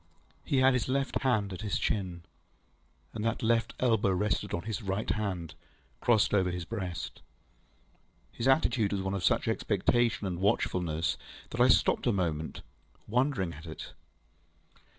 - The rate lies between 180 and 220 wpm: No, average, 150 wpm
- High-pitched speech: No, low, 105 Hz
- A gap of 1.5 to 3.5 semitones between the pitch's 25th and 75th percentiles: No, average, 4.3 semitones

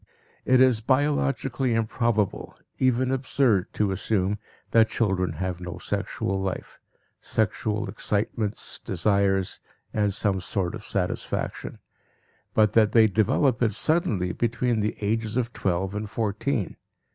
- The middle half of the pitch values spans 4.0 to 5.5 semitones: No, average, 3.4 semitones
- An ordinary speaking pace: No, slow, 125 wpm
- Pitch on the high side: No, low, 105 Hz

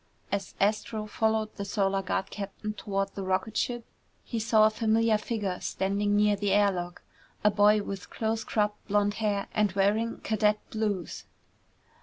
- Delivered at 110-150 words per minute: No, average, 160 wpm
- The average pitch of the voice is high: Yes, high, 210 Hz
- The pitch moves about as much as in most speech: No, narrow, 1.7 semitones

